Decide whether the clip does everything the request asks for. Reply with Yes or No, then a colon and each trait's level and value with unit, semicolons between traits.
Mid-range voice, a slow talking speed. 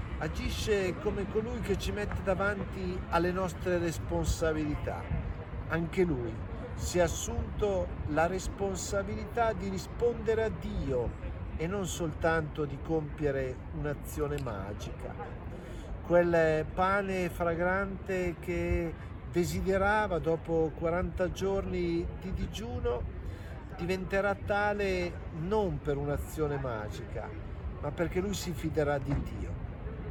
Yes: medium, 155 Hz; slow, 100 wpm